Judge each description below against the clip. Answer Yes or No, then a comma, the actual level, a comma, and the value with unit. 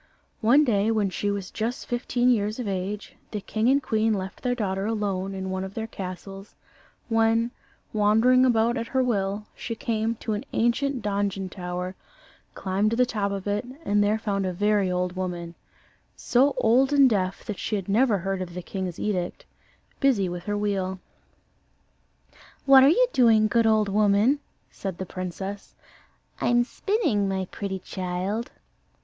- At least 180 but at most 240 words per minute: No, average, 165 wpm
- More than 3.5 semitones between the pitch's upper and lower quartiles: No, average, 3.2 semitones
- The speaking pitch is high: Yes, high, 205 Hz